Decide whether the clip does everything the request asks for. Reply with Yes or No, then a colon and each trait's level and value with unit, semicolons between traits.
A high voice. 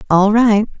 Yes: high, 210 Hz